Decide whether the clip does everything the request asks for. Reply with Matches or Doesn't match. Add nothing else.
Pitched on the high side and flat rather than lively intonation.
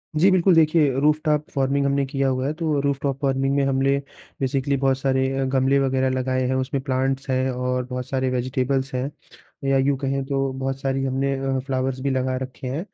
Doesn't match